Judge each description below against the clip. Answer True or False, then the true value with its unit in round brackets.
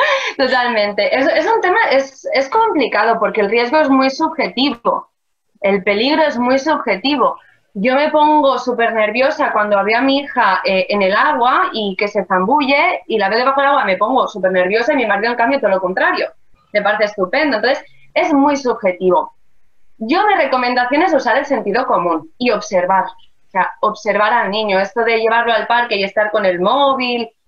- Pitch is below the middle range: False (235 Hz)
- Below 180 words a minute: False (190 wpm)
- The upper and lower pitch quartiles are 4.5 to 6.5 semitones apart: True (5.2 semitones)